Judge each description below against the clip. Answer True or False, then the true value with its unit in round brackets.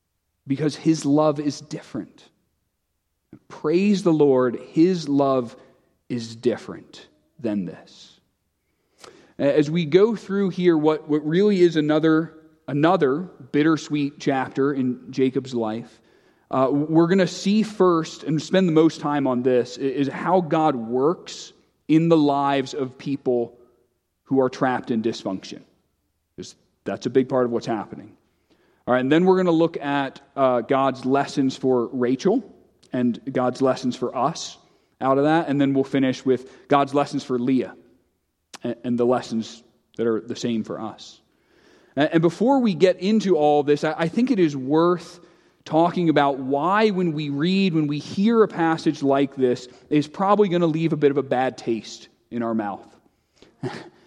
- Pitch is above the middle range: False (140 Hz)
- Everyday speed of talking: True (165 wpm)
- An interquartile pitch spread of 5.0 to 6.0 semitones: False (4.4 semitones)